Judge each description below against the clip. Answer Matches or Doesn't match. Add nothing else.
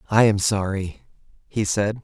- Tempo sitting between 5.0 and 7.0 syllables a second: Doesn't match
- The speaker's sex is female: Doesn't match